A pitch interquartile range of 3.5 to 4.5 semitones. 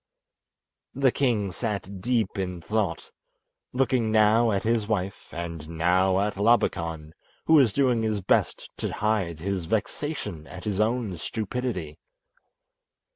Yes: average, 4.2 semitones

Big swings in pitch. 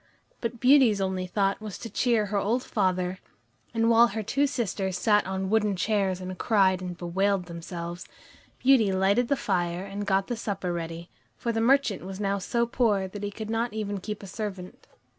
No: average, 3.3 semitones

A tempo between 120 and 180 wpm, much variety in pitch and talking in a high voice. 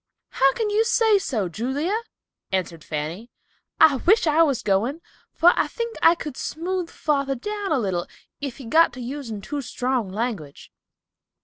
Yes: average, 165 wpm; wide, 7.4 semitones; very high, 275 Hz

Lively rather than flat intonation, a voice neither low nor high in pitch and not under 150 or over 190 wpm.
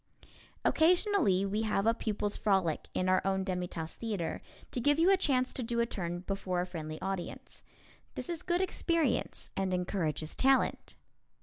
No: wide, 6.3 semitones; high, 200 Hz; average, 170 wpm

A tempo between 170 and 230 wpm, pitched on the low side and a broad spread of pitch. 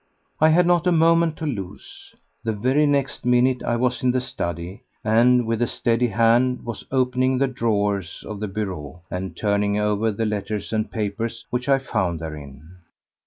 No: average, 175 wpm; low, 115 Hz; average, 4.0 semitones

